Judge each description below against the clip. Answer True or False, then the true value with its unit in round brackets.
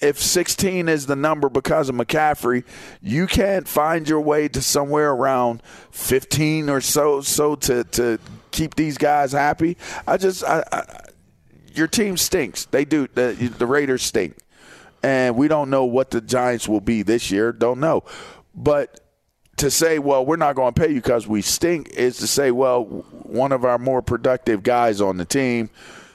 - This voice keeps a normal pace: True (180 wpm)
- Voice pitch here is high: False (140 Hz)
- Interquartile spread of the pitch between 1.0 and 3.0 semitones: False (3.8 semitones)